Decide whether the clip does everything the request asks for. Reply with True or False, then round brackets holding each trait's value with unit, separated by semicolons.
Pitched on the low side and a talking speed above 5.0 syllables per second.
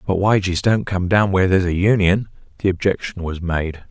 True (95 Hz; 5.6 syllables/s)